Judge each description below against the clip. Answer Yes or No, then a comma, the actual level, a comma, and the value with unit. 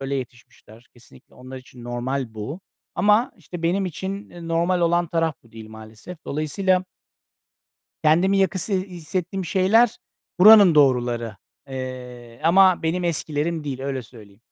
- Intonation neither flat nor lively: No, wide, 6.7 semitones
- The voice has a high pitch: No, medium, 155 Hz